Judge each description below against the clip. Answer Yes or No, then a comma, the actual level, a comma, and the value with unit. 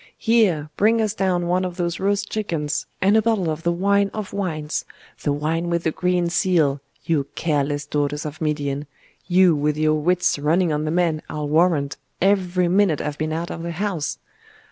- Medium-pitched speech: Yes, medium, 170 Hz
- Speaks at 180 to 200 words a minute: Yes, average, 190 wpm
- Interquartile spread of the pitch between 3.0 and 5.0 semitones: Yes, average, 3.6 semitones